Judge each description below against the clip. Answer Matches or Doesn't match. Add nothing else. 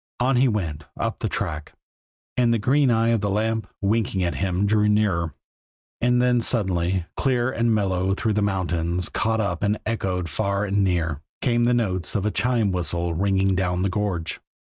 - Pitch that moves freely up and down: Doesn't match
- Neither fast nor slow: Matches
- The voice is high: Doesn't match